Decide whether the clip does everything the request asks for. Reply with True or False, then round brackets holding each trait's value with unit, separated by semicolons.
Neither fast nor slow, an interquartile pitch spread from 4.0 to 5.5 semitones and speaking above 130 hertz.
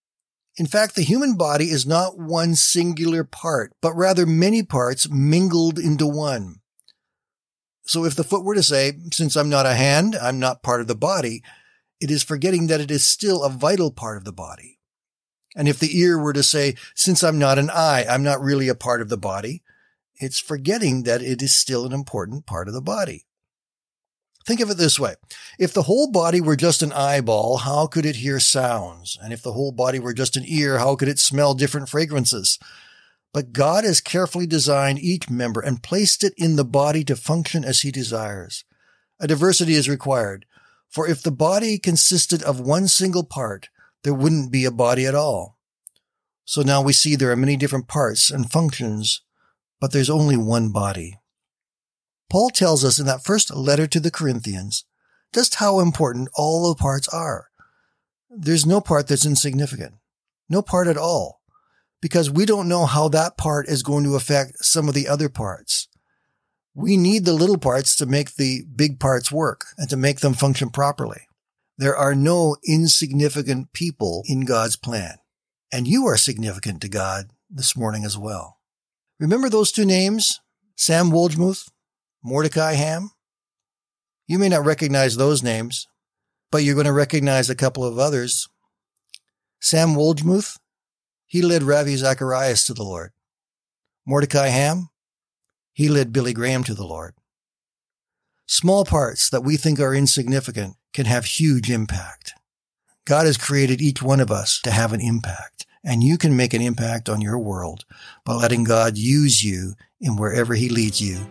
True (175 wpm; 4.7 semitones; 140 Hz)